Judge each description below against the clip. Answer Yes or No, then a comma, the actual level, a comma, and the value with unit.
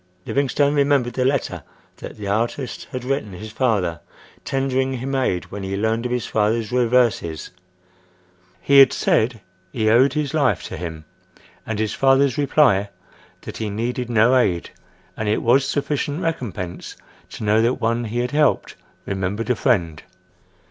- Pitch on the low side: Yes, low, 115 Hz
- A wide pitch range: No, average, 4.9 semitones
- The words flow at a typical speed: Yes, average, 155 wpm